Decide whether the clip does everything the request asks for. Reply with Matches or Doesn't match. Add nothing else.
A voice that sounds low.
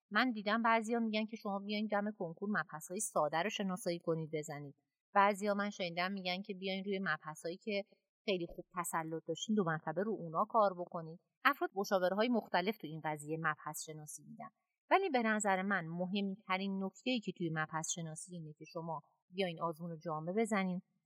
Doesn't match